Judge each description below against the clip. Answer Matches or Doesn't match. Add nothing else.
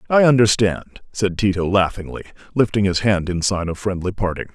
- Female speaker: Doesn't match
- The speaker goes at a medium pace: Matches